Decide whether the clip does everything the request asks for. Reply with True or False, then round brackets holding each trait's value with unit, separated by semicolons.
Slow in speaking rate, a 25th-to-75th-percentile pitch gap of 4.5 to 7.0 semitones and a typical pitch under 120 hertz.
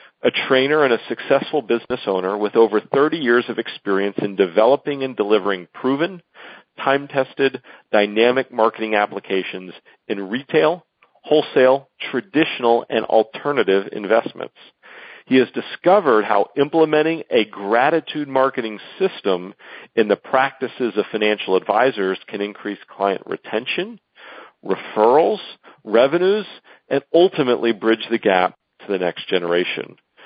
False (115 wpm; 5.4 semitones; 125 Hz)